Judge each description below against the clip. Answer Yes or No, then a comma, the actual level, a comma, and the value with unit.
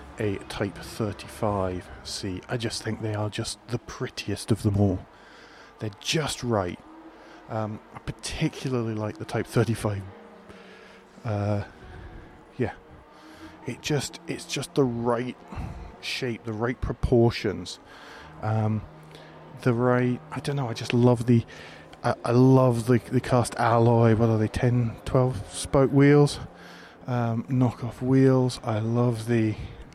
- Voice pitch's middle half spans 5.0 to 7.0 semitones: No, average, 2.9 semitones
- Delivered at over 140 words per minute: No, slow, 135 wpm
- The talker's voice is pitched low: Yes, low, 115 Hz